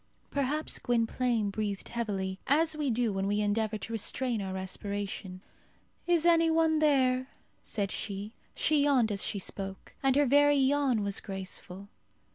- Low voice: No, high, 230 Hz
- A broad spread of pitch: Yes, wide, 6.0 semitones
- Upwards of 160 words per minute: No, average, 150 wpm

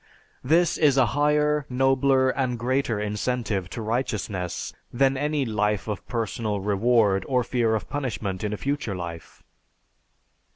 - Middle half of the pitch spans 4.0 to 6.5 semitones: Yes, average, 4.4 semitones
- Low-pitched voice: Yes, low, 120 Hz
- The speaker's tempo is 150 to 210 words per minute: No, slow, 135 wpm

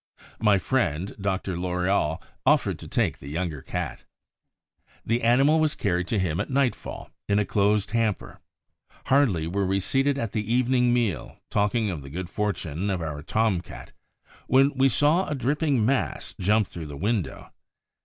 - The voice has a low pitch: Yes, low, 105 Hz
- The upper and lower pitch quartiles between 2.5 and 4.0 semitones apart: No, wide, 5.6 semitones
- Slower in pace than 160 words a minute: No, average, 165 wpm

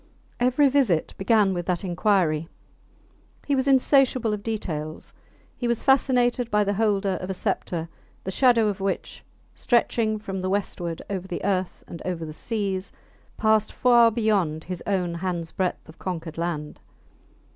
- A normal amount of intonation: Yes, average, 4.7 semitones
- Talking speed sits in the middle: Yes, average, 155 wpm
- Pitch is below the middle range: No, high, 195 Hz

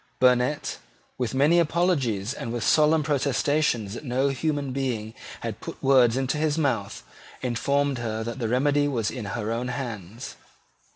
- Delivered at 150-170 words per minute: Yes, average, 155 wpm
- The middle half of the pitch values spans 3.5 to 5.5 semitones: Yes, average, 3.8 semitones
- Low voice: Yes, low, 130 Hz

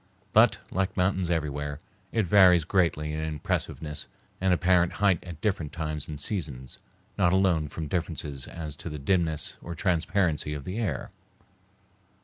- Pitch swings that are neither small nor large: Yes, average, 3.4 semitones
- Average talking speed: Yes, average, 145 wpm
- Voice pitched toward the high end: No, very low, 85 Hz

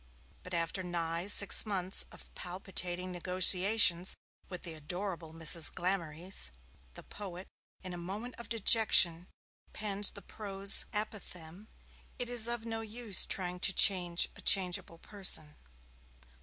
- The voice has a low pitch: No, medium, 185 Hz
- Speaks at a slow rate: Yes, slow, 130 wpm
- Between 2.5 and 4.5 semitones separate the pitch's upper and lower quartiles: Yes, average, 2.9 semitones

